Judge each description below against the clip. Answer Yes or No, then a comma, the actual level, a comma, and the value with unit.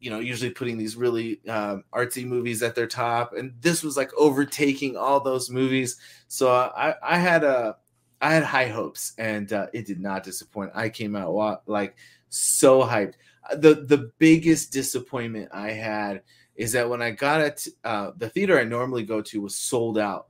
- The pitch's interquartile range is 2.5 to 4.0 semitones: Yes, average, 3.6 semitones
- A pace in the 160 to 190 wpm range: Yes, average, 185 wpm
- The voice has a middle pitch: No, low, 120 Hz